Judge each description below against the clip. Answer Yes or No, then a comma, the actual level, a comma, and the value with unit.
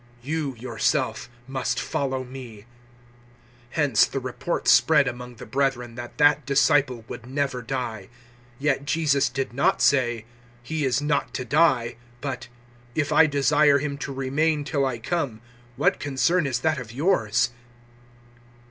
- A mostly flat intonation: No, average, 3.0 semitones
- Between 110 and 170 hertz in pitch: Yes, low, 135 Hz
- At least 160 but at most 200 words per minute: No, average, 145 wpm